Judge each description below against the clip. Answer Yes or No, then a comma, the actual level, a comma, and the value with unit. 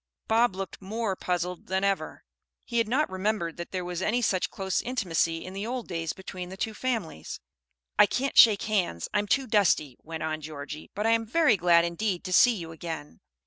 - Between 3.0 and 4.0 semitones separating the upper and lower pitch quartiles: No, average, 4.7 semitones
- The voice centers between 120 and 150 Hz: No, high, 190 Hz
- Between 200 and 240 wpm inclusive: Yes, fast, 205 wpm